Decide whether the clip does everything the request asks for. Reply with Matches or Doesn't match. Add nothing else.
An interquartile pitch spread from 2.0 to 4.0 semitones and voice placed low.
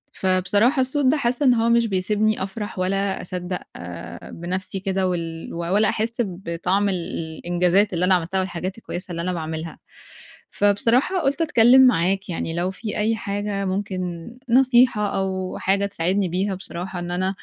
Doesn't match